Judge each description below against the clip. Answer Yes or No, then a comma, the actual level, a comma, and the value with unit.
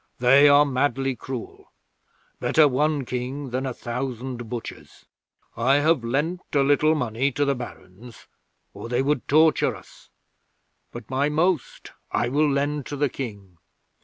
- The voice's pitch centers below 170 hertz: Yes, low, 135 Hz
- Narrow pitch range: No, average, 3.1 semitones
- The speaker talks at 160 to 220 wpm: No, average, 145 wpm